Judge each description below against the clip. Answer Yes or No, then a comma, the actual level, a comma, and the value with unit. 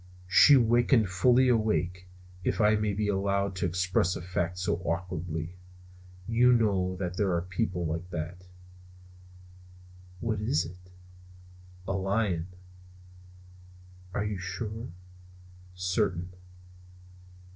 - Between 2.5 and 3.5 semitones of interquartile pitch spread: Yes, average, 3.1 semitones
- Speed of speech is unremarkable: No, slow, 115 wpm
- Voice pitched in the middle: No, very low, 95 Hz